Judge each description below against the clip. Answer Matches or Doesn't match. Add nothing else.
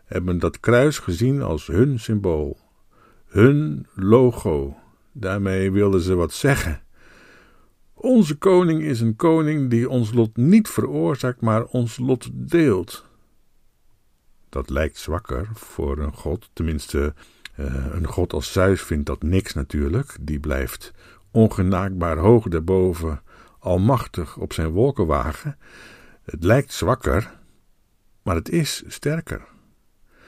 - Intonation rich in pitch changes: Matches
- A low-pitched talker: Matches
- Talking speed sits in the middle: Doesn't match